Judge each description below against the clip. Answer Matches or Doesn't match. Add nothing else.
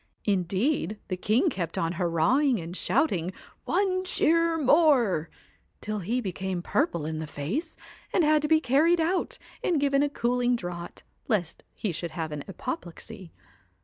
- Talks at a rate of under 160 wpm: Matches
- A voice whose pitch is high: Matches